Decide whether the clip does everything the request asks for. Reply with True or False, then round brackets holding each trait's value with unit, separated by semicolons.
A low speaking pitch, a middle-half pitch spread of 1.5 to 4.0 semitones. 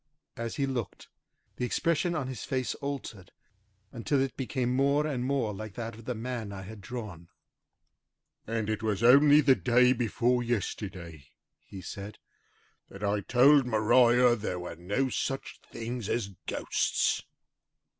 True (120 Hz; 3.7 semitones)